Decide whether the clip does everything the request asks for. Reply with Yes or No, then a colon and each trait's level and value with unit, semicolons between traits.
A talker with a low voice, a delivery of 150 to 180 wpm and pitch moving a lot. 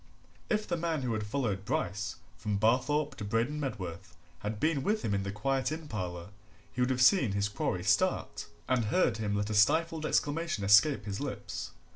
No: low, 115 Hz; average, 190 wpm; wide, 6.4 semitones